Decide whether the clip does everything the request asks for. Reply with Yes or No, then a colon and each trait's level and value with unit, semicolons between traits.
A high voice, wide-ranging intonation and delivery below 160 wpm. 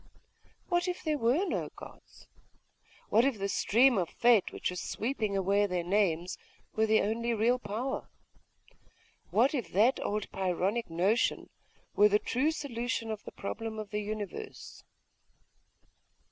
No: high, 220 Hz; average, 3.5 semitones; average, 145 wpm